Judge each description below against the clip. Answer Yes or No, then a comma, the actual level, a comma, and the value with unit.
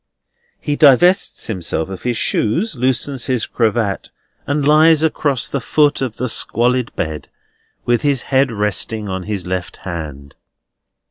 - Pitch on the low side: Yes, low, 120 Hz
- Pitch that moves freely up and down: Yes, wide, 6.2 semitones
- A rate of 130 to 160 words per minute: Yes, average, 140 wpm